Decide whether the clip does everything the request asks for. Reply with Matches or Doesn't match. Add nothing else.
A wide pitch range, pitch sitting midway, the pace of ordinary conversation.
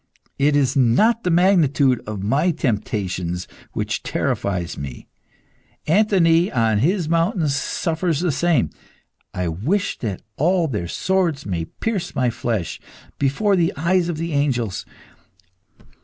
Doesn't match